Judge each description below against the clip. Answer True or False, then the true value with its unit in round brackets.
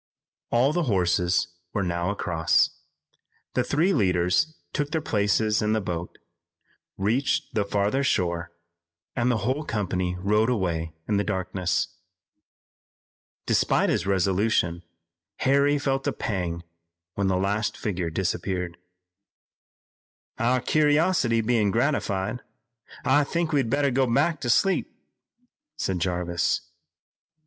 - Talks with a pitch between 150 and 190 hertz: False (105 Hz)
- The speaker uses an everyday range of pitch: False (6.4 semitones)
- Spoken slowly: True (120 wpm)